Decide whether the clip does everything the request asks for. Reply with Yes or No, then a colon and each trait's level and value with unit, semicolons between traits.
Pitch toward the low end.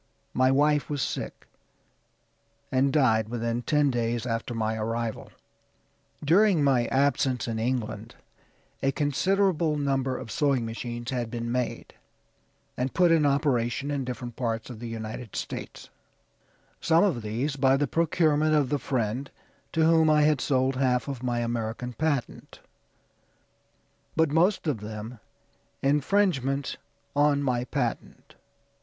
Yes: low, 130 Hz